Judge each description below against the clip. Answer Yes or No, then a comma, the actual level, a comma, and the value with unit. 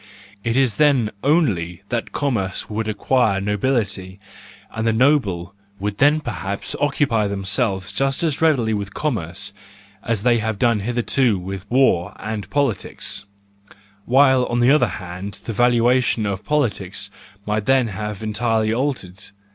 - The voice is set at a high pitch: No, low, 110 Hz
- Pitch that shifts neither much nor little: Yes, average, 4.4 semitones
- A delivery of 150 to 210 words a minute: No, average, 140 wpm